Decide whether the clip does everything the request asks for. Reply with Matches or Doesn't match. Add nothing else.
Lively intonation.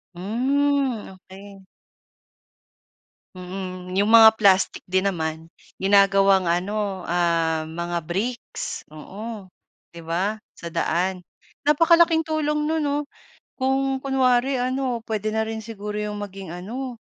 Matches